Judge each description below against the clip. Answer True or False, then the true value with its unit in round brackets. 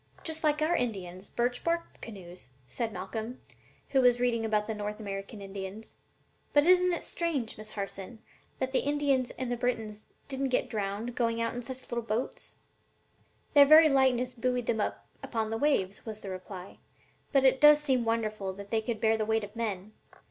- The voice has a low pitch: False (230 Hz)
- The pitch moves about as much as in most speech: True (3.8 semitones)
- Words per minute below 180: False (190 wpm)